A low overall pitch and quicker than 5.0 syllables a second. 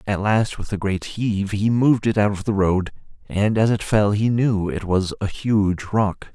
No: low, 105 Hz; 4.5 syllables/s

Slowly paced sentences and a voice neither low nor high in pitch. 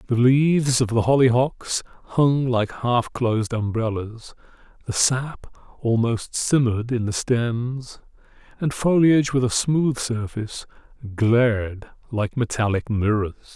No: slow, 120 wpm; low, 120 Hz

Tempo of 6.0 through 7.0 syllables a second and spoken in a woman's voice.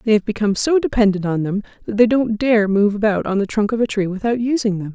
Yes: 6.3 syllables/s; female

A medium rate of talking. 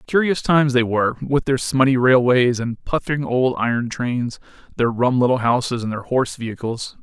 Yes: average, 180 wpm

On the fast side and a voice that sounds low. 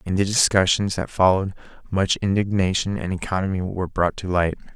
No: average, 165 wpm; very low, 95 Hz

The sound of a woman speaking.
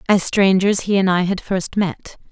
Yes: female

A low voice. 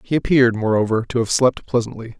Yes: low, 120 Hz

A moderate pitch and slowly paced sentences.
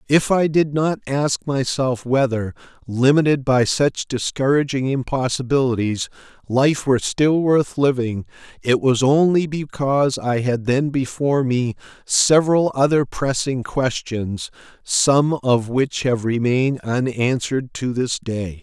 No: low, 130 Hz; slow, 125 wpm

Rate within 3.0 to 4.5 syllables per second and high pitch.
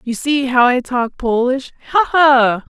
Yes: 3.8 syllables/s; very high, 260 Hz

